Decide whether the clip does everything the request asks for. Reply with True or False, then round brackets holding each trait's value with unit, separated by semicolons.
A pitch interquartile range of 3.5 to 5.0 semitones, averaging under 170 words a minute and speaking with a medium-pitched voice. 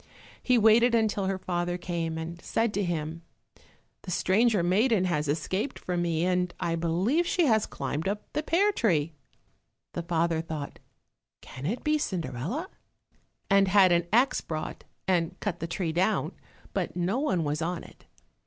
True (4.7 semitones; 160 wpm; 180 Hz)